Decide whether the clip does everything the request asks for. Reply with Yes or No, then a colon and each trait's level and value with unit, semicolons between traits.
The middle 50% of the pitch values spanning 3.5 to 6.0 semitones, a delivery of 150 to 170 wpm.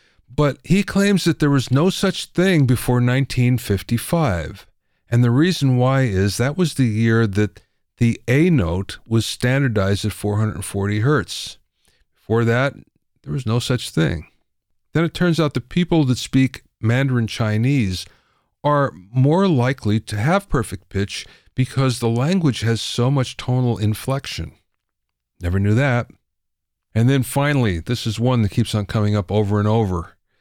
Yes: average, 4.9 semitones; average, 155 wpm